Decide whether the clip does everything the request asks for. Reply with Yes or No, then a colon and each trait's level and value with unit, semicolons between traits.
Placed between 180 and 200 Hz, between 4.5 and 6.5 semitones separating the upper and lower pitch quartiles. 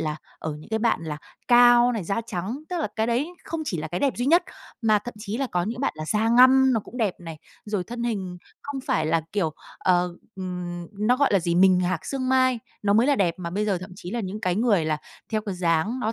No: high, 210 Hz; wide, 5.4 semitones